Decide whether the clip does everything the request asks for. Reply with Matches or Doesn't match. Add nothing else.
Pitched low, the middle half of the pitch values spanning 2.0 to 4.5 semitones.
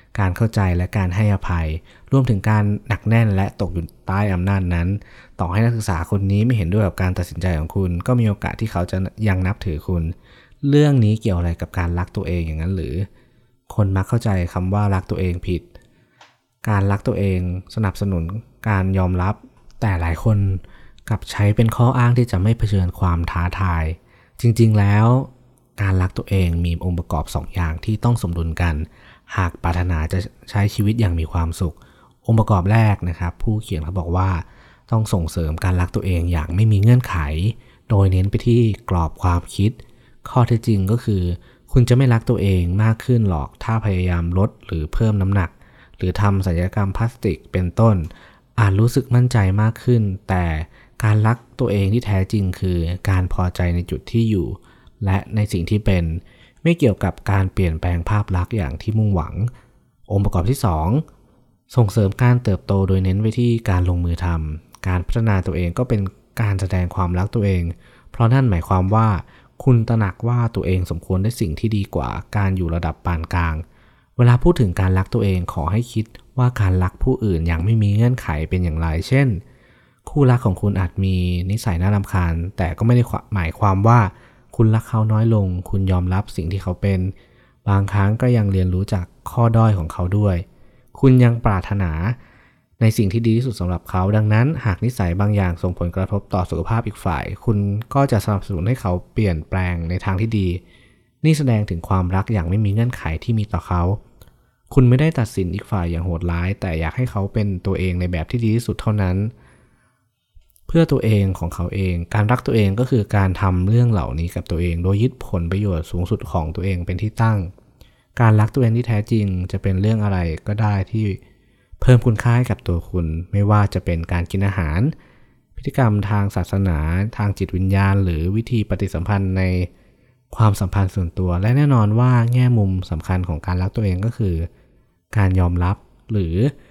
Matches